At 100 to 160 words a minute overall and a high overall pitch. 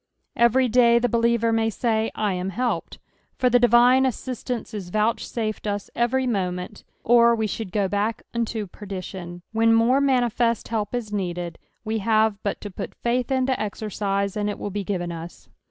No: average, 170 wpm; high, 220 Hz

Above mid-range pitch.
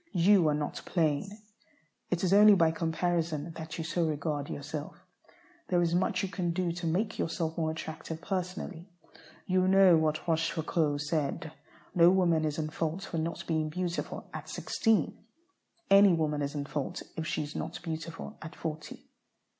No: medium, 165 Hz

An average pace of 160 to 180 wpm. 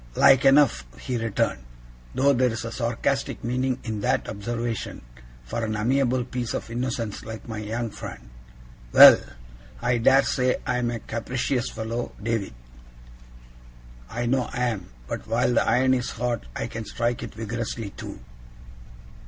No: average, 150 wpm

